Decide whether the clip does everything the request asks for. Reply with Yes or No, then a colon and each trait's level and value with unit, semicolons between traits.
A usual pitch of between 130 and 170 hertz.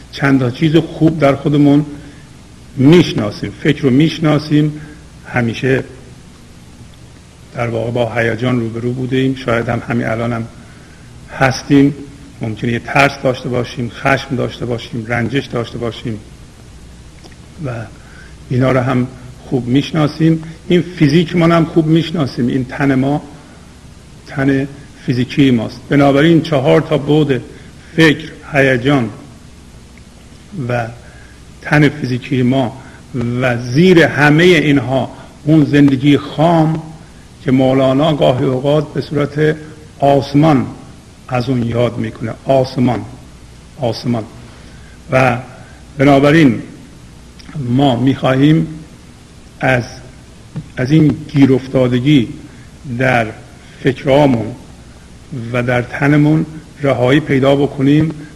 Yes: low, 135 Hz